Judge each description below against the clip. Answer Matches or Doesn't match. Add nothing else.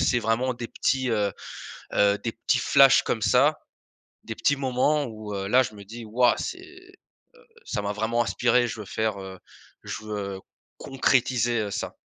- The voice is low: Matches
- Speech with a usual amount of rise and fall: Matches